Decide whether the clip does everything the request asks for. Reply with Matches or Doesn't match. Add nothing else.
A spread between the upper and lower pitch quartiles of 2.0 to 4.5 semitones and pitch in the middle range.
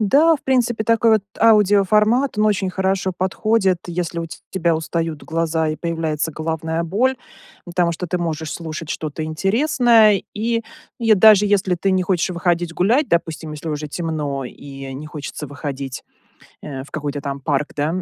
Doesn't match